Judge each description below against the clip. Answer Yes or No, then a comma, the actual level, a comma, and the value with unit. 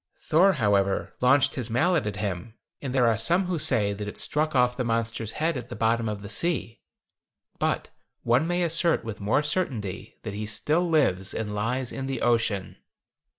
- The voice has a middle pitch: No, low, 120 Hz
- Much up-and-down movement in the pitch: Yes, wide, 6.1 semitones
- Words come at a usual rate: Yes, average, 190 wpm